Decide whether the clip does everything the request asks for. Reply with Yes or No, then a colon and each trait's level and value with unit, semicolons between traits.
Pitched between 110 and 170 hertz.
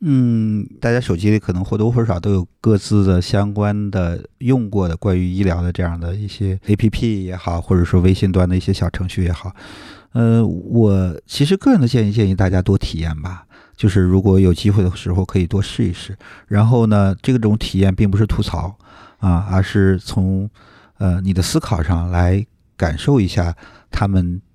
No: very low, 95 Hz